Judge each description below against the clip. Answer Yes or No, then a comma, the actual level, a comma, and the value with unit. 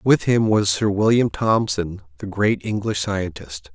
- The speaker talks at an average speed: Yes, average, 160 wpm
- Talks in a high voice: No, low, 105 Hz